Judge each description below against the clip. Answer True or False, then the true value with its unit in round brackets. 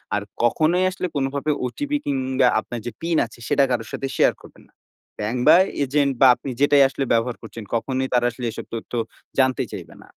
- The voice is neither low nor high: False (130 Hz)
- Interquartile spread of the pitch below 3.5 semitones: True (2.9 semitones)